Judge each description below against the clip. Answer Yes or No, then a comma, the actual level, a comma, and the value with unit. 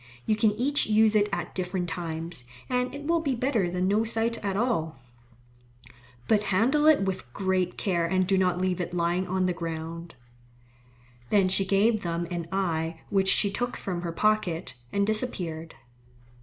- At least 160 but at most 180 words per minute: Yes, average, 170 wpm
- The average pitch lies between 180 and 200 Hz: Yes, high, 190 Hz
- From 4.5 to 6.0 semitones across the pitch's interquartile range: No, average, 3.9 semitones